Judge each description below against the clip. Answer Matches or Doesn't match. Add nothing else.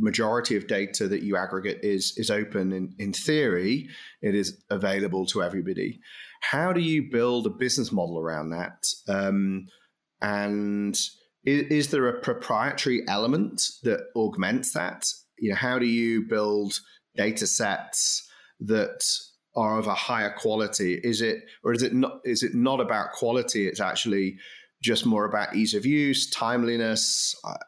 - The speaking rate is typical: Matches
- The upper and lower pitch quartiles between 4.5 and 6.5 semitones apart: Matches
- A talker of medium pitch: Doesn't match